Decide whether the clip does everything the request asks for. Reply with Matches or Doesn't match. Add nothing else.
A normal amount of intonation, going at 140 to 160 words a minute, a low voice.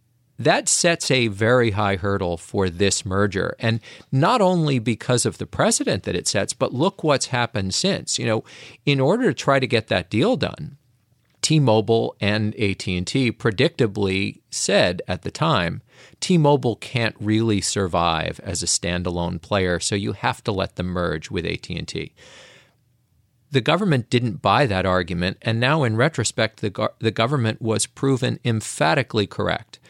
Matches